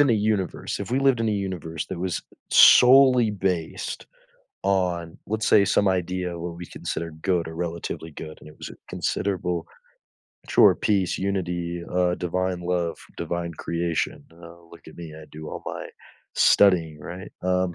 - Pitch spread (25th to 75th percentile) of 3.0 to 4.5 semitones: No, narrow, 2.5 semitones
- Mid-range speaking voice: No, very low, 90 Hz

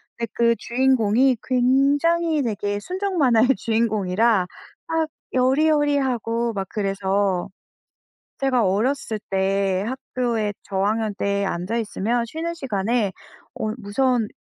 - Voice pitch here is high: Yes, high, 230 Hz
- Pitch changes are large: No, average, 4.6 semitones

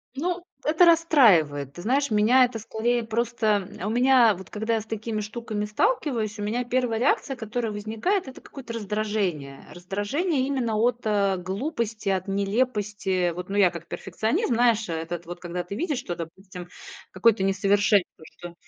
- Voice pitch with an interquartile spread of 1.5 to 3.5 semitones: No, average, 4.1 semitones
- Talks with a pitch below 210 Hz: No, high, 215 Hz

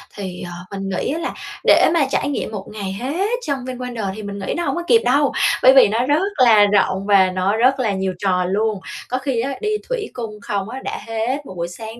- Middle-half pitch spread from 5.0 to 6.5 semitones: Yes, average, 5.3 semitones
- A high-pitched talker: Yes, high, 225 Hz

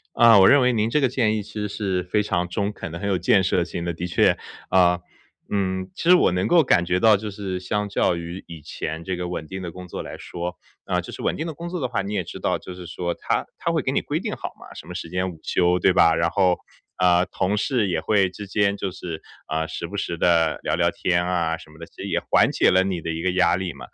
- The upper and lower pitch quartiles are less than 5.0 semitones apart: Yes, average, 2.9 semitones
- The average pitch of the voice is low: Yes, very low, 90 Hz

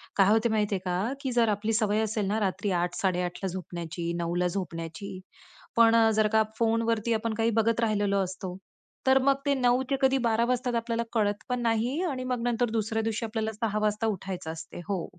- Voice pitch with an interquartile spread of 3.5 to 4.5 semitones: No, average, 3.1 semitones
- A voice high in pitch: Yes, high, 220 Hz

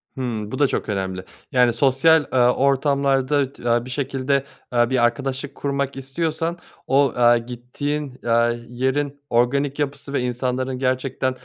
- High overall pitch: No, low, 130 Hz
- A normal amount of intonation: No, narrow, 2.3 semitones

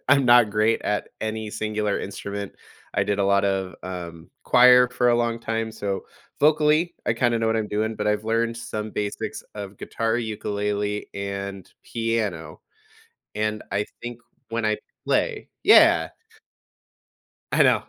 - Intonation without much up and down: Yes, narrow, 2.3 semitones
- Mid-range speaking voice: No, low, 110 Hz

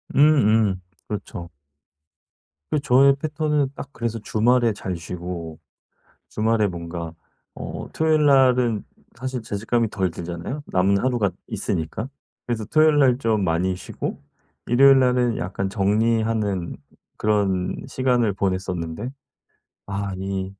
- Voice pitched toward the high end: No, low, 110 Hz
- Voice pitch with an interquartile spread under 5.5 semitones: Yes, average, 5.1 semitones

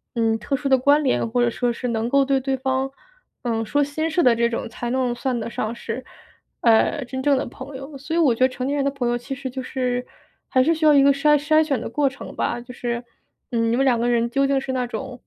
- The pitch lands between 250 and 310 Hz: Yes, very high, 260 Hz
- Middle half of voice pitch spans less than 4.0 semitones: Yes, narrow, 2.5 semitones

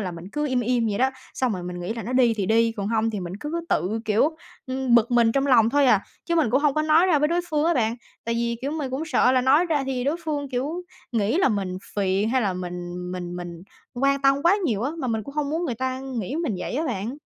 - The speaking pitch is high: Yes, very high, 250 Hz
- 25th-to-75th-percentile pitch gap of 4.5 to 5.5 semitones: Yes, average, 5.2 semitones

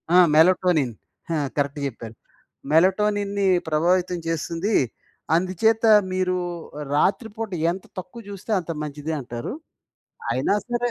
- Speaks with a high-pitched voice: No, medium, 180 Hz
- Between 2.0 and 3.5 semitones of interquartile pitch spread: No, average, 4.7 semitones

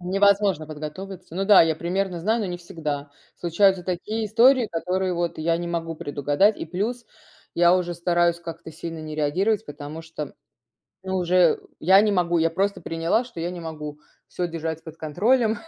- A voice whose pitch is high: No, medium, 175 Hz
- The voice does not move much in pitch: No, average, 3.1 semitones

